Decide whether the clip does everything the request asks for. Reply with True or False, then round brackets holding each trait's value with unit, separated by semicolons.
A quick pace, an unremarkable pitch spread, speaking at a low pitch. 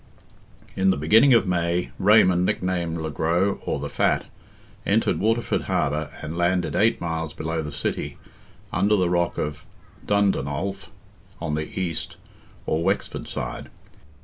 False (140 wpm; 3.4 semitones; 85 Hz)